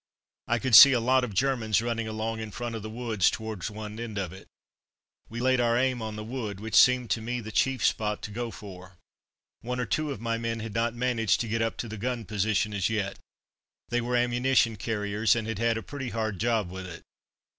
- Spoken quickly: Yes, fast, 230 wpm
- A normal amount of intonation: No, narrow, 2.2 semitones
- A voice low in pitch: Yes, low, 115 Hz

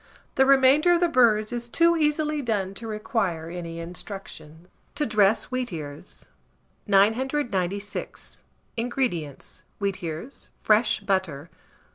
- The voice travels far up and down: Yes, wide, 6.5 semitones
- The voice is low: No, high, 215 Hz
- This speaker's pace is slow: Yes, slow, 105 wpm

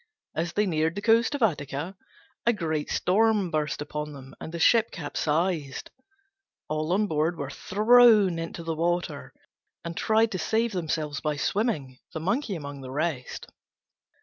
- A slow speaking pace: No, average, 155 wpm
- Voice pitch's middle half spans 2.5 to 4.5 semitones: No, wide, 5.6 semitones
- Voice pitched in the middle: Yes, medium, 165 Hz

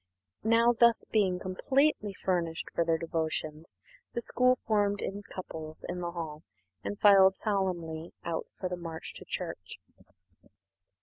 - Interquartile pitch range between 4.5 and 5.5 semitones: No, average, 3.8 semitones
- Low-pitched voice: No, medium, 180 Hz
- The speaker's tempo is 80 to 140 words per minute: Yes, slow, 135 wpm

